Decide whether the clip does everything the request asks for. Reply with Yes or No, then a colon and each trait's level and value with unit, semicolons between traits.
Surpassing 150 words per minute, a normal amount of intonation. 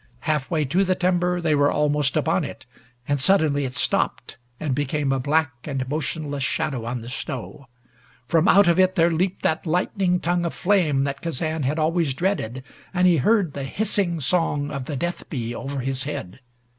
Yes: average, 190 wpm; average, 4.3 semitones